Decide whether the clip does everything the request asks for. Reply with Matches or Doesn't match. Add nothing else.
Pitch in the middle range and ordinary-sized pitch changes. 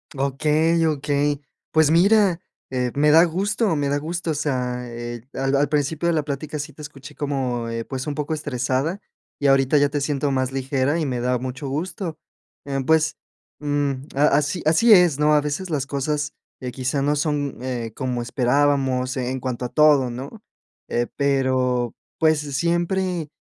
Matches